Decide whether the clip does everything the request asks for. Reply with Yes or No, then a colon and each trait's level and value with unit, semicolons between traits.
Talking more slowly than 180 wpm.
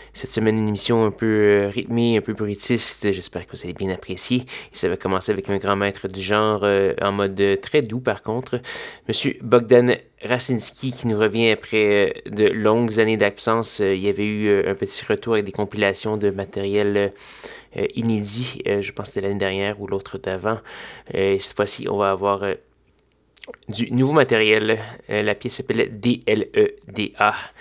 No: average, 200 wpm